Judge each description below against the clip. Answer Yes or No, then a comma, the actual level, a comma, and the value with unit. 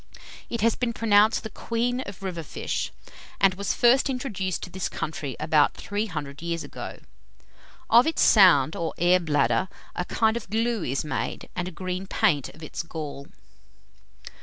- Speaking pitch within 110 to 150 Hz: No, medium, 185 Hz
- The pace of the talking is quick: No, average, 165 wpm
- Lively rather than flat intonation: Yes, wide, 5.7 semitones